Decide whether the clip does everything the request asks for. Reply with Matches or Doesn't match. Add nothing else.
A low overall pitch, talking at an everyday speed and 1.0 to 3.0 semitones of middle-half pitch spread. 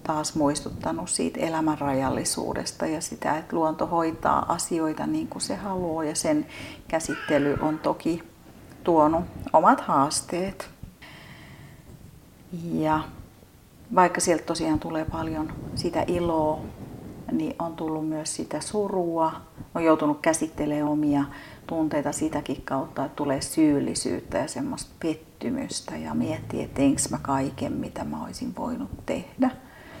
Doesn't match